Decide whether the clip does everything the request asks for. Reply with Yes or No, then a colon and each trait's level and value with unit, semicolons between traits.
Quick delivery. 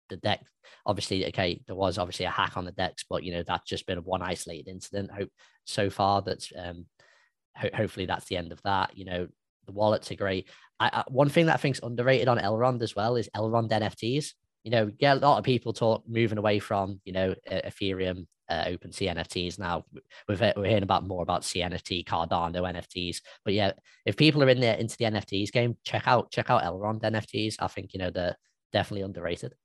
Yes: fast, 220 wpm